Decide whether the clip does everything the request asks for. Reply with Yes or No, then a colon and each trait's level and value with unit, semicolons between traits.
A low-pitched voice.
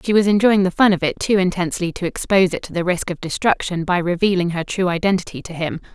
No: medium, 180 Hz